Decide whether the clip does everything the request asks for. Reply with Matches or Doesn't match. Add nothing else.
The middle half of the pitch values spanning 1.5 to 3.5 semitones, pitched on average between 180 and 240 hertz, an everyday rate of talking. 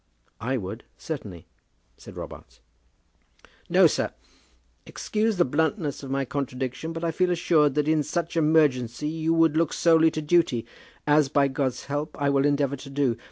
Doesn't match